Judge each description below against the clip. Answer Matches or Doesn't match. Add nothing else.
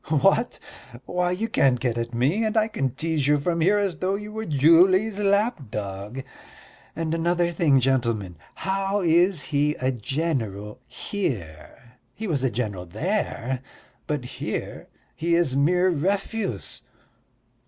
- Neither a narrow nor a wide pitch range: Doesn't match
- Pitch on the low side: Doesn't match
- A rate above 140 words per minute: Doesn't match